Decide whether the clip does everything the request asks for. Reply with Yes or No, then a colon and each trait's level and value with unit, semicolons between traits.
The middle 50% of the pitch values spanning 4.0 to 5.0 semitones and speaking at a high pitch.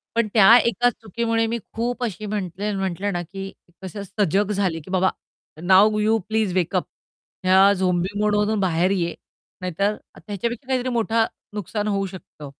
No: average, 2.8 semitones; high, 200 Hz